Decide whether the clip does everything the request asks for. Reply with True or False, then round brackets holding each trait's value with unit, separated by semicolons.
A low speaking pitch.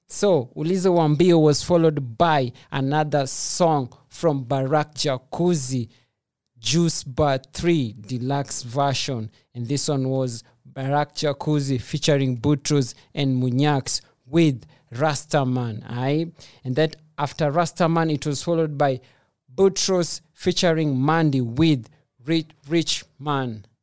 False (145 Hz)